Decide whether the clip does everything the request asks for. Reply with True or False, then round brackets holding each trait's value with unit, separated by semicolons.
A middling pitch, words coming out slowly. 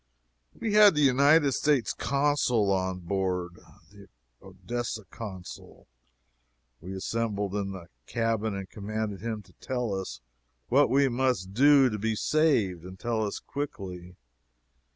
False (110 Hz; 130 wpm)